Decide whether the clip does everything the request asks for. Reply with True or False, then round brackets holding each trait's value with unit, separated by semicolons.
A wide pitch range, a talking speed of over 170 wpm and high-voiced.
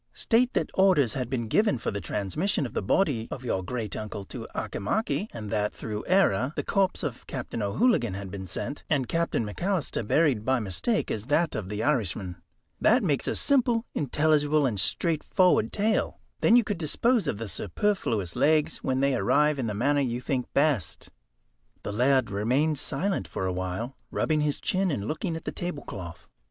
False (8.1 semitones; 185 wpm; 135 Hz)